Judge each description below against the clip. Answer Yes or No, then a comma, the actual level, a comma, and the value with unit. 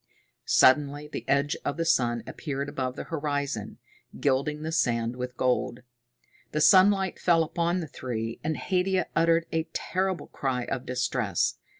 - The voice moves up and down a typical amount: Yes, average, 4.6 semitones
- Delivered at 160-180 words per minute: No, average, 150 wpm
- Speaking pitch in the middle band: Yes, medium, 145 Hz